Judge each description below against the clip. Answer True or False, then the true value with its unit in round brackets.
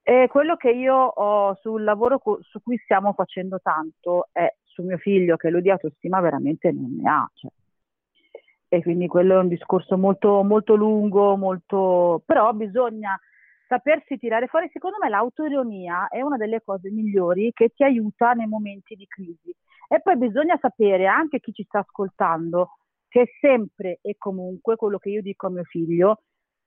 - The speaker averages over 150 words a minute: True (170 wpm)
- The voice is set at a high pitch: True (210 Hz)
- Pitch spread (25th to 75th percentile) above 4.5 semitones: True (4.9 semitones)